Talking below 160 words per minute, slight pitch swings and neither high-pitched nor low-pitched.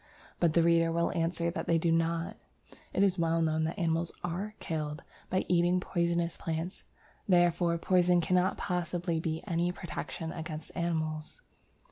Yes: average, 150 wpm; narrow, 1.3 semitones; medium, 170 Hz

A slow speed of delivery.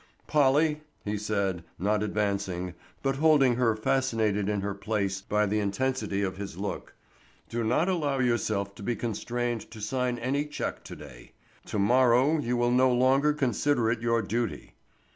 No: average, 160 wpm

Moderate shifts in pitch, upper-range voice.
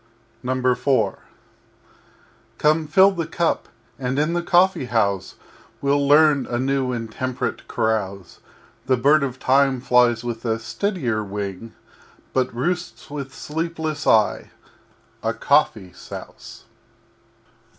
No: average, 4.9 semitones; low, 130 Hz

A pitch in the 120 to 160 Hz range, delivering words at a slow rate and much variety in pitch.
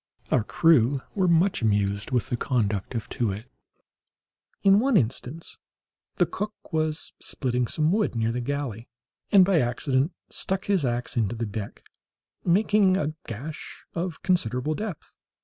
No: medium, 140 Hz; average, 150 wpm; wide, 7.3 semitones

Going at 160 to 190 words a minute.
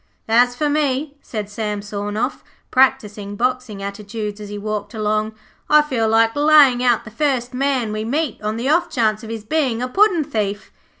Yes: average, 180 wpm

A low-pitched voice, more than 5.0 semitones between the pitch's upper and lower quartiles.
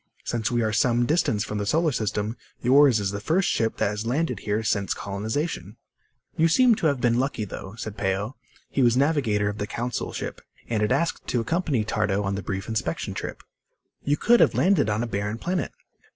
Yes: low, 115 Hz; wide, 5.5 semitones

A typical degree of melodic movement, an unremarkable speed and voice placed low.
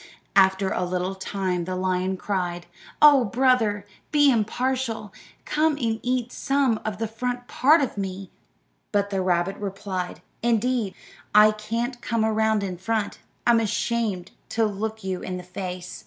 No: average, 3.9 semitones; average, 150 wpm; high, 215 Hz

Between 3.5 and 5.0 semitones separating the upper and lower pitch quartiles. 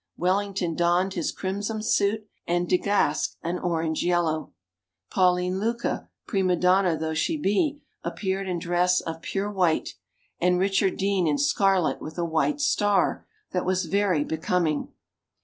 No: narrow, 2.6 semitones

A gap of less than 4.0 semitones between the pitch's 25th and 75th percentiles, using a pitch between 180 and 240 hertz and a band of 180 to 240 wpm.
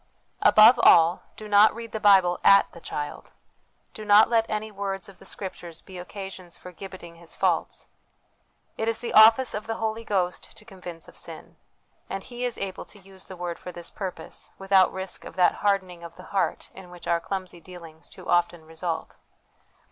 Yes: average, 3.2 semitones; high, 190 Hz; average, 190 wpm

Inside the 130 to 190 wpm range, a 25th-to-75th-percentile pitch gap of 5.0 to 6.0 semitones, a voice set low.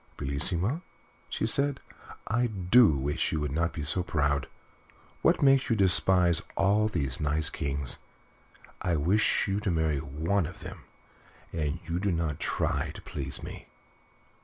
Yes: average, 150 wpm; average, 5.3 semitones; very low, 85 Hz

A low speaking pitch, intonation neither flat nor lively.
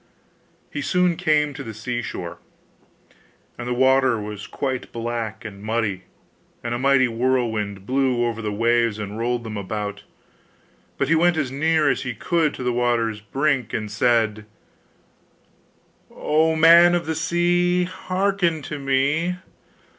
No: low, 125 Hz; wide, 6.0 semitones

